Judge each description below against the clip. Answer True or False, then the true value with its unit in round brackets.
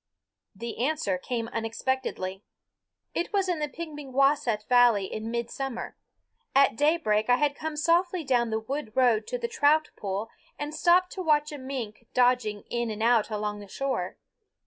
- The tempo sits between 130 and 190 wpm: True (160 wpm)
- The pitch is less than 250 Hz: False (255 Hz)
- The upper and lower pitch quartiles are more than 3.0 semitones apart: True (5.2 semitones)